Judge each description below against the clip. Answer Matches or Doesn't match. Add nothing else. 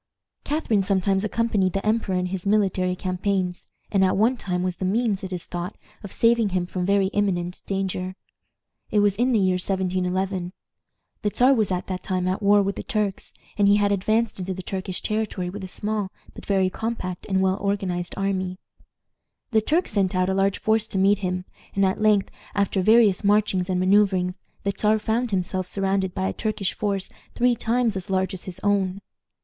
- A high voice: Matches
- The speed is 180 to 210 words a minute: Matches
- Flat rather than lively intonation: Matches